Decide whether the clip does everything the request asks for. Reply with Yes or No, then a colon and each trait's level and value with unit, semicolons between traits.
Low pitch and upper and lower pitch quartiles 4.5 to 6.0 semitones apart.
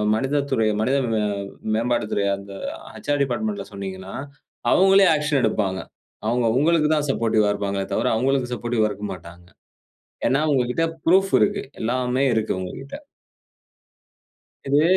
Yes: low, 125 Hz; wide, 5.6 semitones